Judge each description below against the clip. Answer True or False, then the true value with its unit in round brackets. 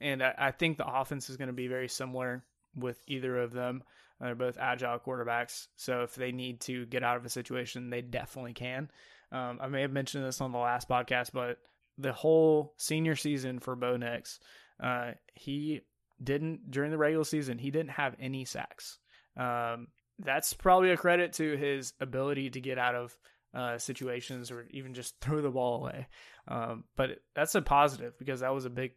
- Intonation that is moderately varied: False (2.3 semitones)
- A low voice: True (130 Hz)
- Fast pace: False (195 wpm)